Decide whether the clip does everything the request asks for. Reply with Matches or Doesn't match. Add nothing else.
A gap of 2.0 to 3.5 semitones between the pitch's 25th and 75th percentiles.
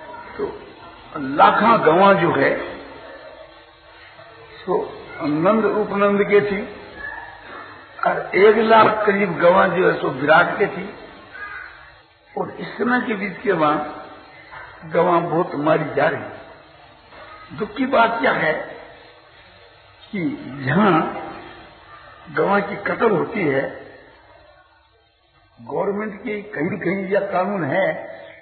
Doesn't match